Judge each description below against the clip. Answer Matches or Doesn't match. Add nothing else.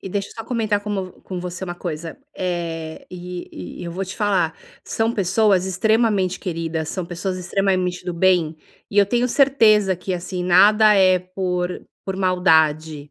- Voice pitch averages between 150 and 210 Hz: Matches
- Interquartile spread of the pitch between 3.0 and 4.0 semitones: Doesn't match